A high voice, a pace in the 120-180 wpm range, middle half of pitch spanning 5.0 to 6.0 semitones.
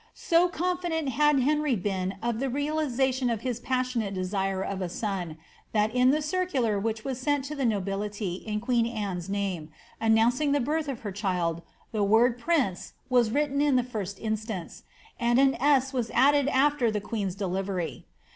Yes: high, 235 Hz; average, 175 wpm; wide, 5.4 semitones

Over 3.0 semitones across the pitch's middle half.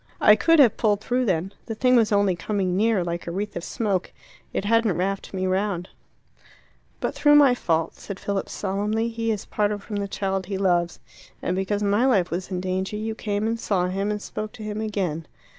No: average, 2.7 semitones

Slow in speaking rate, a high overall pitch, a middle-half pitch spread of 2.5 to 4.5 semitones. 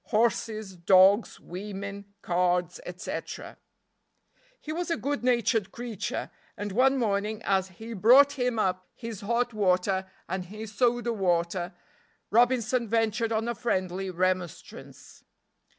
Yes: slow, 120 wpm; high, 210 Hz; average, 4.0 semitones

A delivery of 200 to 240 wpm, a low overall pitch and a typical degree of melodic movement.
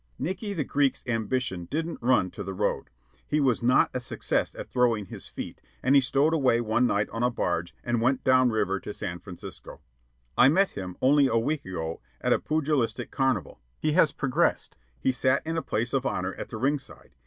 Yes: fast, 205 wpm; low, 125 Hz; average, 4.8 semitones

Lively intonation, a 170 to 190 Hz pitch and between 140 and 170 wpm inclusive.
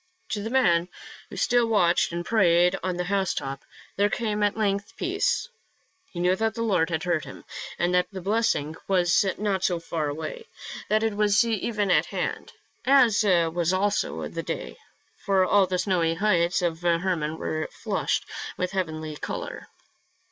No: average, 3.7 semitones; medium, 185 Hz; average, 165 wpm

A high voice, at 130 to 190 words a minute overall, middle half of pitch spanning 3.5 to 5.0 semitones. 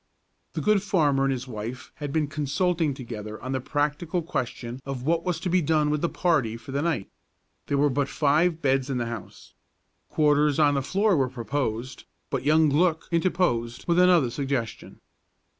No: medium, 145 Hz; average, 180 wpm; average, 4.2 semitones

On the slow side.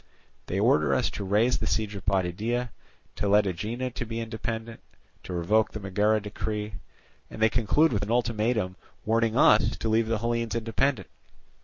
No: average, 165 wpm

